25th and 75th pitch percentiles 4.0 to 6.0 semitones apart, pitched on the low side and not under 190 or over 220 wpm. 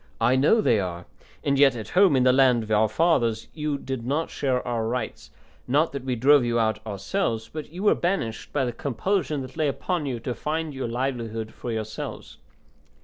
Yes: average, 4.6 semitones; low, 130 Hz; fast, 205 wpm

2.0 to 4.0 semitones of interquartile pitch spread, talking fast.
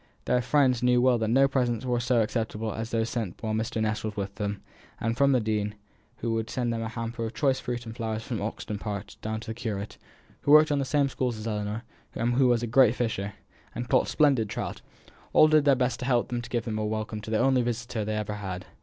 Yes: narrow, 2.5 semitones; fast, 245 wpm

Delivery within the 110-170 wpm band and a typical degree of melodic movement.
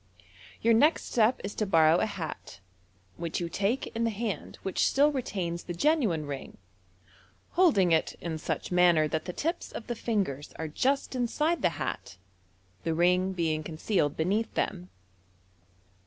No: average, 155 wpm; wide, 6.0 semitones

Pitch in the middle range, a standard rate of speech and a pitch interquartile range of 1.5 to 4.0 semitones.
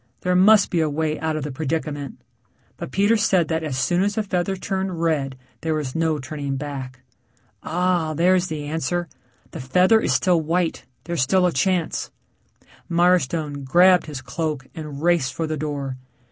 Yes: medium, 160 Hz; average, 175 wpm; average, 3.6 semitones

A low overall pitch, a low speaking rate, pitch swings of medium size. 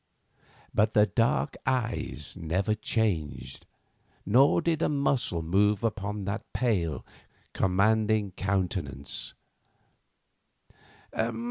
Yes: low, 105 Hz; slow, 85 wpm; average, 3.6 semitones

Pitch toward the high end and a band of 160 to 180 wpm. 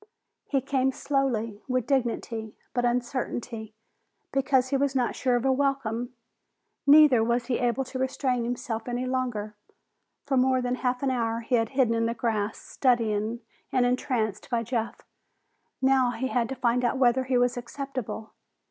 Yes: high, 245 Hz; average, 165 wpm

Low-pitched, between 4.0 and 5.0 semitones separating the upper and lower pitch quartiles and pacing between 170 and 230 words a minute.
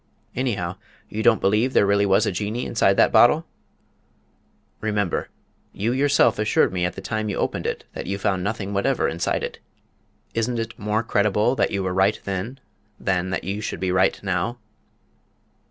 No: low, 105 Hz; average, 2.9 semitones; average, 175 wpm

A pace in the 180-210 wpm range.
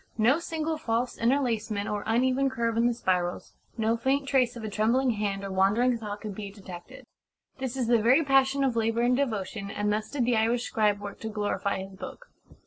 Yes: fast, 205 wpm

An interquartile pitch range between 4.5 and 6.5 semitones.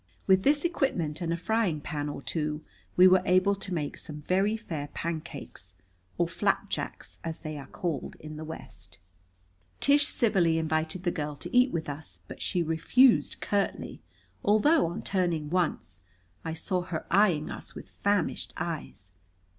No: average, 4.1 semitones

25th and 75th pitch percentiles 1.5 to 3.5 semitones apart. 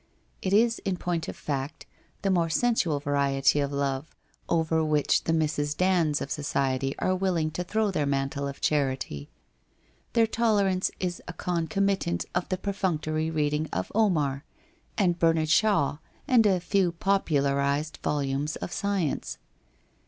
No: average, 4.7 semitones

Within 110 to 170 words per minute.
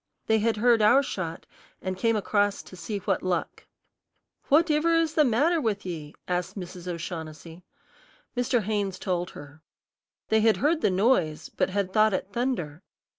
Yes: average, 165 wpm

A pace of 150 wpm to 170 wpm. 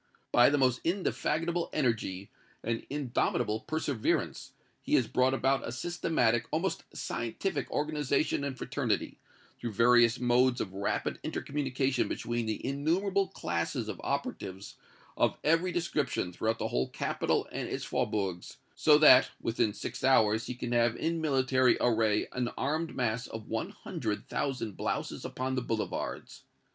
No: average, 140 wpm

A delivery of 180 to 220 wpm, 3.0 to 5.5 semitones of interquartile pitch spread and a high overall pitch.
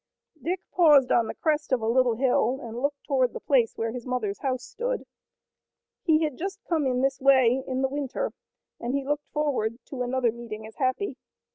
Yes: average, 195 wpm; average, 3.3 semitones; very high, 260 Hz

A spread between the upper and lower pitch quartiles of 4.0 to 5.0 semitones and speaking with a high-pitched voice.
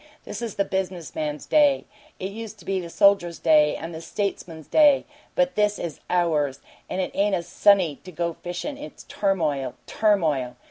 No: average, 4.4 semitones; medium, 180 Hz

